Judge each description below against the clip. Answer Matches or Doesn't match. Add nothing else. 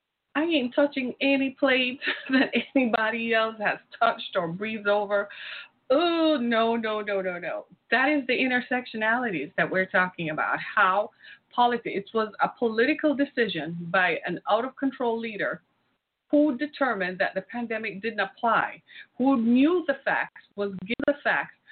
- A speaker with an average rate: Matches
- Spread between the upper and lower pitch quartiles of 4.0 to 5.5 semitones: Matches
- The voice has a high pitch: Matches